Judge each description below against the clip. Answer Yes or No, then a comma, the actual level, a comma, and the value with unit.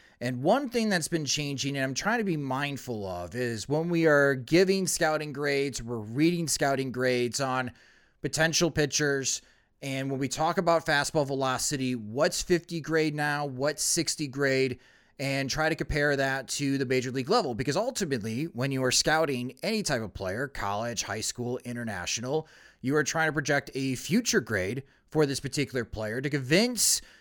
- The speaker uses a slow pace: No, average, 175 wpm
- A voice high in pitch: No, medium, 140 Hz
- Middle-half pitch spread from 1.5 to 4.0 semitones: Yes, average, 3.6 semitones